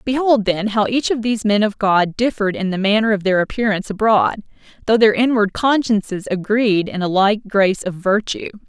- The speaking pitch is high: Yes, high, 210 Hz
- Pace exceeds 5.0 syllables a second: Yes, 5.5 syllables/s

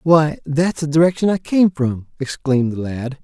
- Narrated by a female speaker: No, male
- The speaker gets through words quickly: No, average, 185 wpm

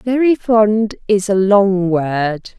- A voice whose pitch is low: No, high, 205 Hz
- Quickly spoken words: No, average, 140 wpm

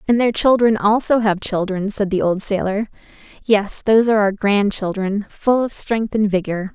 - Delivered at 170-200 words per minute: Yes, average, 185 wpm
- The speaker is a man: No, female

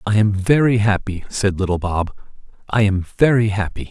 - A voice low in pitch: Yes, low, 105 Hz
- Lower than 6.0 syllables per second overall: Yes, 5.2 syllables/s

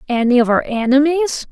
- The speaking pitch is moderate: No, very high, 265 Hz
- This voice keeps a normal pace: Yes, average, 160 wpm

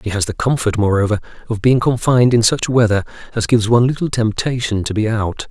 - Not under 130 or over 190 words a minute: No, fast, 205 wpm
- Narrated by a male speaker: Yes, male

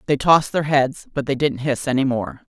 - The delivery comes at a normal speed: No, fast, 235 wpm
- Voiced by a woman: Yes, female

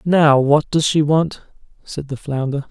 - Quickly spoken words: No, average, 175 wpm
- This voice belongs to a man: Yes, male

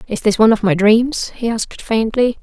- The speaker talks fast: Yes, fast, 220 wpm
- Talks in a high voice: Yes, high, 220 Hz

